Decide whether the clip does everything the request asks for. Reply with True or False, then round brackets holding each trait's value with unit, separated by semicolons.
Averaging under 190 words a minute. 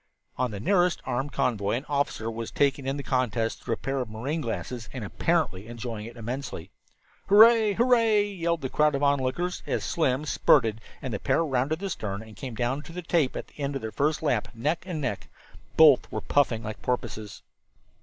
False (200 wpm)